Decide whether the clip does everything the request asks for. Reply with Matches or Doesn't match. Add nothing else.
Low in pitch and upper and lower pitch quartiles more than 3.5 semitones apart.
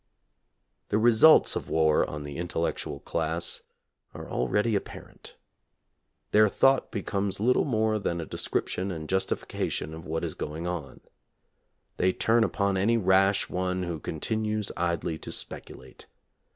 Matches